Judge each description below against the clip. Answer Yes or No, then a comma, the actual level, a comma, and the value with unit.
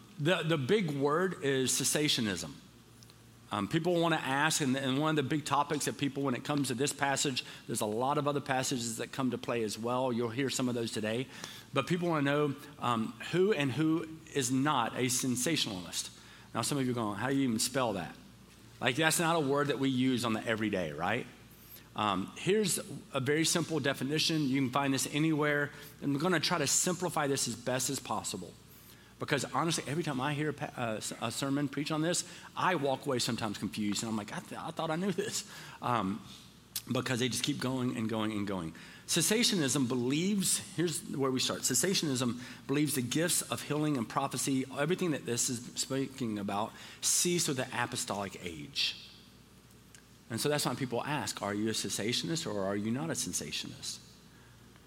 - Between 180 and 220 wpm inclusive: Yes, average, 200 wpm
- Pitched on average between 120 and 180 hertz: Yes, low, 135 Hz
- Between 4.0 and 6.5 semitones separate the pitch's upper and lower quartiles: Yes, average, 4.3 semitones